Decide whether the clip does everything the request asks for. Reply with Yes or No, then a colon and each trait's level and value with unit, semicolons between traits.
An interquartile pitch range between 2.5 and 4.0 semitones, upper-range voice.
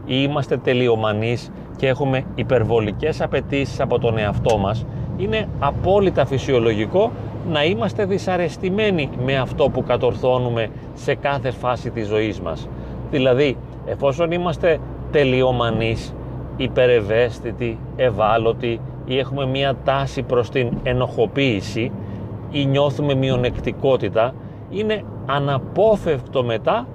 No: average, 3.3 semitones; low, 130 Hz